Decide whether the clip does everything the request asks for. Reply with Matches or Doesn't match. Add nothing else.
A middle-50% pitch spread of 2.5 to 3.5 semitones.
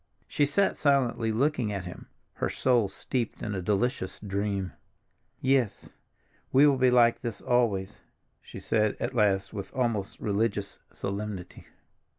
Doesn't match